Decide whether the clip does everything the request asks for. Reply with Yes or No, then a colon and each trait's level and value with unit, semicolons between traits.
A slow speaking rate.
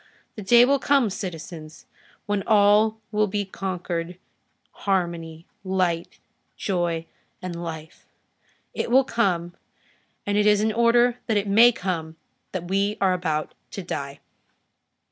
Yes: slow, 130 wpm